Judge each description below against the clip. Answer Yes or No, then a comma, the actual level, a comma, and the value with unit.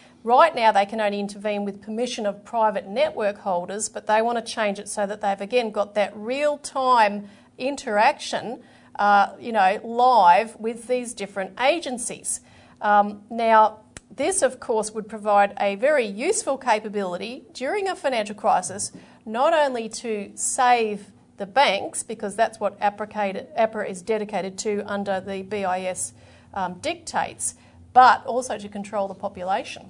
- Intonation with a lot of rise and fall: No, average, 3.1 semitones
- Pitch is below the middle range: No, high, 215 Hz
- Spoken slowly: No, average, 145 wpm